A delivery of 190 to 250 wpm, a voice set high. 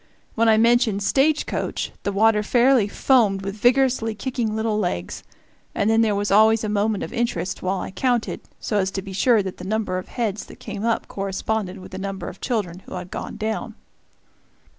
Yes: average, 200 wpm; high, 215 Hz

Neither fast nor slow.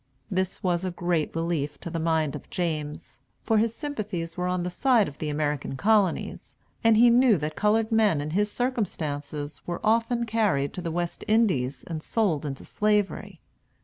Yes: average, 180 wpm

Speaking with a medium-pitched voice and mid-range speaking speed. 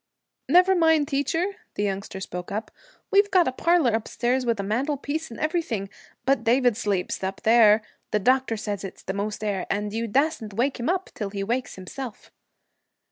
No: high, 235 Hz; average, 180 wpm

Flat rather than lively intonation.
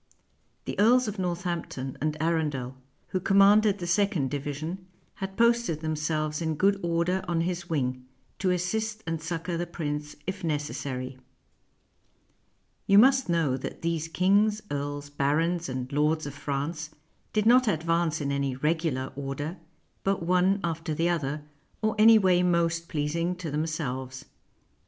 No: average, 3.8 semitones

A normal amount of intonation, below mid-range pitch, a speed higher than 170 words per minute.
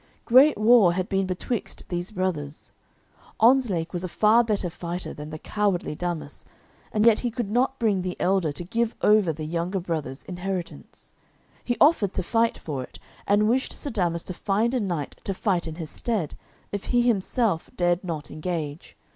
No: average, 4.6 semitones; medium, 185 Hz; average, 180 wpm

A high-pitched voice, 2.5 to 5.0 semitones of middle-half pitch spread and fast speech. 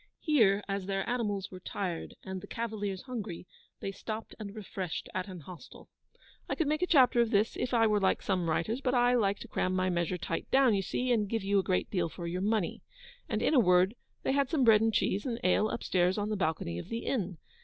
Yes: high, 205 Hz; average, 4.0 semitones; fast, 235 wpm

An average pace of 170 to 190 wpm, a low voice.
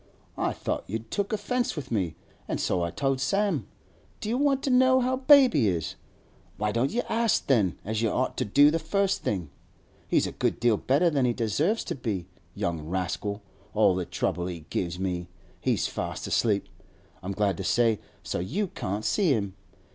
Yes: average, 185 wpm; low, 115 Hz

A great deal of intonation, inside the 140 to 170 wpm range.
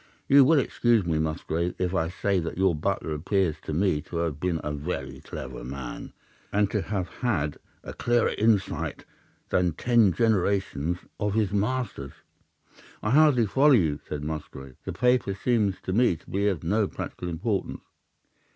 Yes: wide, 5.7 semitones; average, 165 wpm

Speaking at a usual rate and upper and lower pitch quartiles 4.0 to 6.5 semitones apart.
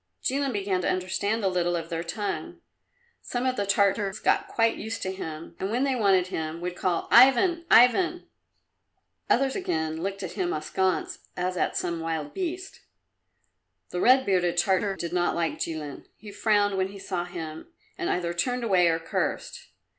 Yes: average, 175 wpm; average, 4.7 semitones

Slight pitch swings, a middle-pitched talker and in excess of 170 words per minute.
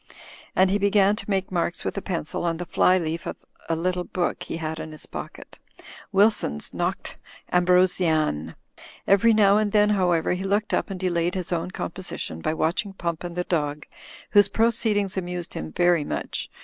No: average, 3.0 semitones; medium, 180 Hz; average, 185 wpm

